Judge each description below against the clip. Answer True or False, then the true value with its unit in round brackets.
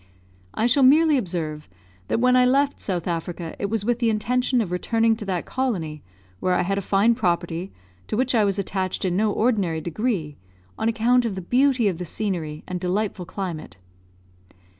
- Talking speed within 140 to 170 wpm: False (185 wpm)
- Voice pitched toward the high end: True (200 Hz)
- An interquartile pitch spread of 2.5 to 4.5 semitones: False (5.1 semitones)